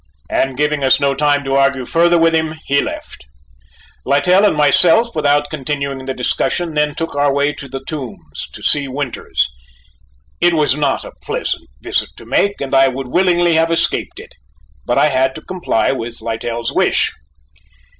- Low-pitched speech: No, medium, 145 Hz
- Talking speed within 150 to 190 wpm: Yes, average, 175 wpm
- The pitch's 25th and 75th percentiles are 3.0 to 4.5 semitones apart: Yes, average, 3.3 semitones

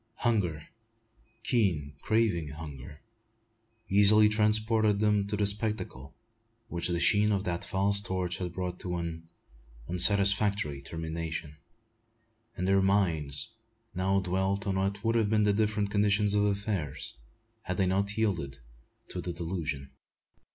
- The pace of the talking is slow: Yes, slow, 130 wpm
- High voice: No, very low, 95 Hz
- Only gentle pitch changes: No, average, 3.7 semitones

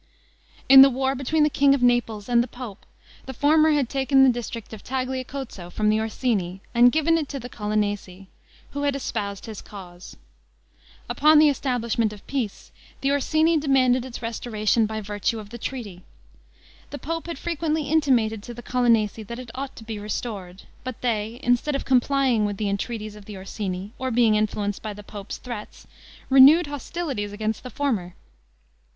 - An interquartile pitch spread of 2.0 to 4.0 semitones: No, average, 4.5 semitones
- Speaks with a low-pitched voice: No, high, 240 Hz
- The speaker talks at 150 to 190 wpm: Yes, average, 175 wpm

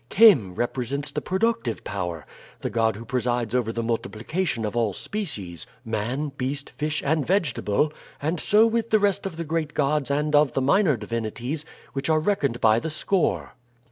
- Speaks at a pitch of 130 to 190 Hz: Yes, medium, 140 Hz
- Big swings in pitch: Yes, wide, 5.8 semitones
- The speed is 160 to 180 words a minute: Yes, average, 170 wpm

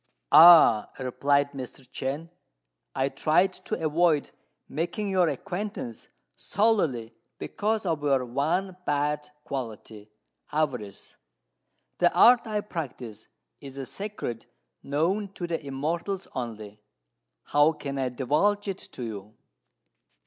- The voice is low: No, medium, 145 Hz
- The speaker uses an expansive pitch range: Yes, wide, 5.8 semitones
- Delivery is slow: Yes, slow, 115 wpm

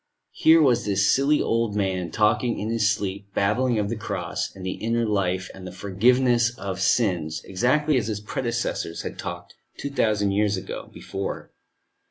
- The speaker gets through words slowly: No, average, 165 wpm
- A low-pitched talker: Yes, low, 105 Hz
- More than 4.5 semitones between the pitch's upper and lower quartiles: No, average, 3.5 semitones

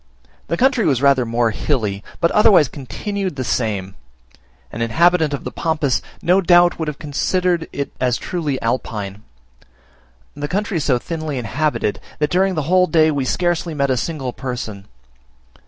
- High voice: No, medium, 145 Hz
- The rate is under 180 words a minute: Yes, average, 160 wpm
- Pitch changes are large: Yes, wide, 5.7 semitones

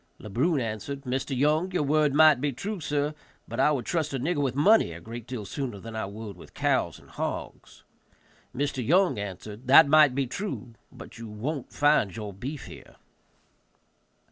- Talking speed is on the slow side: No, average, 185 wpm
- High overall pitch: No, low, 135 Hz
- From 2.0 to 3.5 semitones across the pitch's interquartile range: No, average, 5.0 semitones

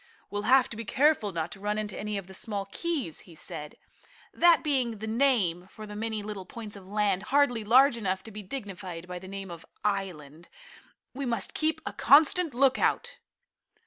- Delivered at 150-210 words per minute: Yes, average, 190 wpm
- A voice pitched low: No, high, 210 Hz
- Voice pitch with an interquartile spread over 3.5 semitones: Yes, average, 5.1 semitones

